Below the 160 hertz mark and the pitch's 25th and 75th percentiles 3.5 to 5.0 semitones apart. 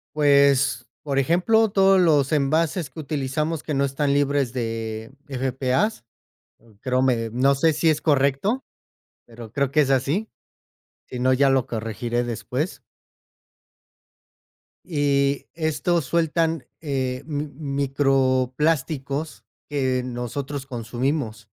No: medium, 140 Hz; average, 3.1 semitones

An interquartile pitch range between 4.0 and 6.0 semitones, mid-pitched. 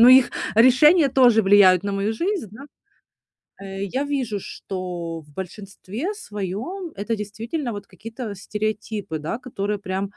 No: average, 4.5 semitones; high, 210 Hz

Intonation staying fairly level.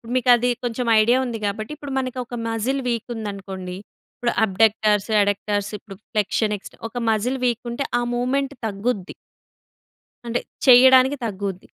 No: average, 3.5 semitones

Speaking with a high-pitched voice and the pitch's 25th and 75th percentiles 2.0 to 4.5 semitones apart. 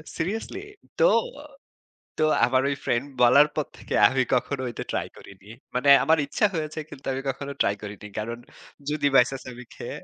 No: low, 135 Hz; average, 3.8 semitones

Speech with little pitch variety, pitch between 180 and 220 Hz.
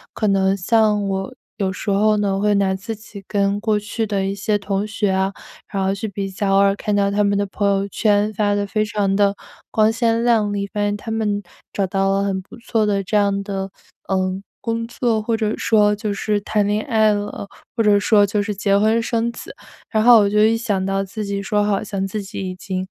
Yes: narrow, 1.5 semitones; high, 205 Hz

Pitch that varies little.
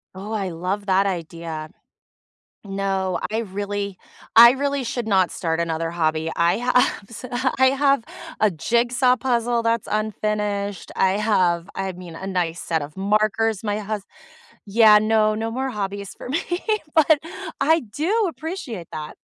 No: average, 4.1 semitones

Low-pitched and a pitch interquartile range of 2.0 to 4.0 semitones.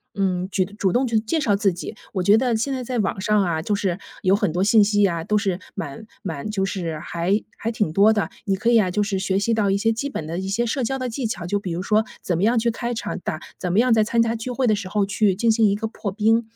No: high, 205 Hz; average, 3.1 semitones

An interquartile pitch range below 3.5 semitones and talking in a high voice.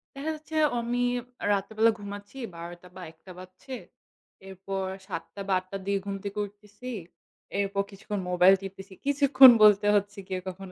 Yes: narrow, 2.4 semitones; high, 200 Hz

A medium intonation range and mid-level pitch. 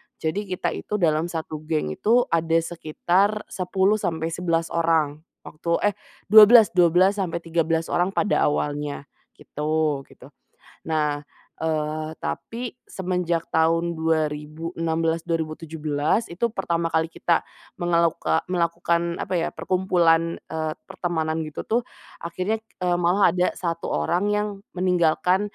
No: narrow, 2.3 semitones; medium, 165 Hz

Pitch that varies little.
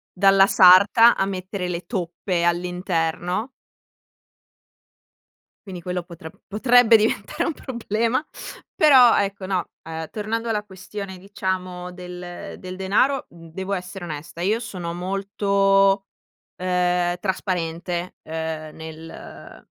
Yes: narrow, 2.3 semitones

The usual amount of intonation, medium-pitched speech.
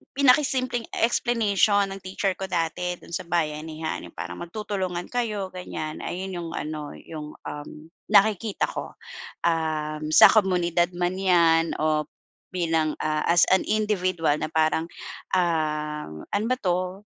Yes: average, 3.8 semitones; medium, 175 Hz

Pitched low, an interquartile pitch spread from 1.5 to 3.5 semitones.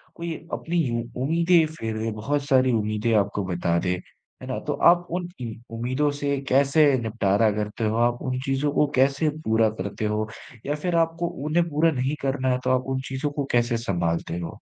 No: low, 130 Hz; average, 5.2 semitones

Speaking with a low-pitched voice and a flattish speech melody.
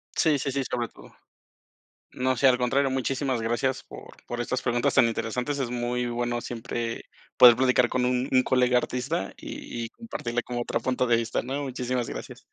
Yes: low, 125 Hz; narrow, 1.5 semitones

